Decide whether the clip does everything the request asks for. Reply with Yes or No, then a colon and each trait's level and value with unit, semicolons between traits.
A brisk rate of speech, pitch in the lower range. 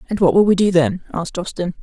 No: fast, 260 wpm; medium, 185 Hz